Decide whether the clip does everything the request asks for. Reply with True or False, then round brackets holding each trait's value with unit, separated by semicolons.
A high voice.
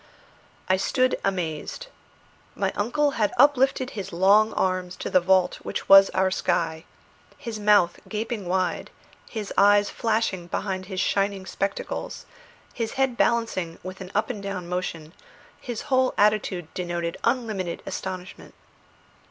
True (195 Hz)